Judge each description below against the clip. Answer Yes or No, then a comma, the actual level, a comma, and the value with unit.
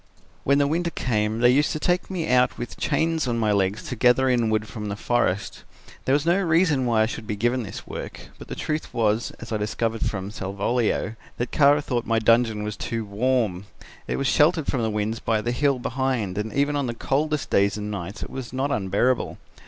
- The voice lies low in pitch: Yes, low, 120 Hz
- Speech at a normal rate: No, fast, 220 wpm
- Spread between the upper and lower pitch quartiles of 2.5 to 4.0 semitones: No, average, 4.5 semitones